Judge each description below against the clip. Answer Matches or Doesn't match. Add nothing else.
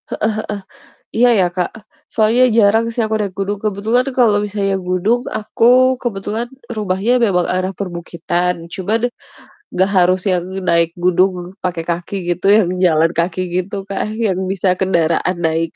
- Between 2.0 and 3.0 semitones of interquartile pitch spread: Doesn't match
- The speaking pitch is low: Doesn't match